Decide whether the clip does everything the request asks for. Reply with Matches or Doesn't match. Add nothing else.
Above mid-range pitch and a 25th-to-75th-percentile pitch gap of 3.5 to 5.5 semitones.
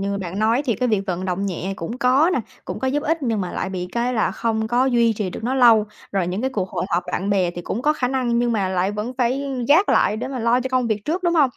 Matches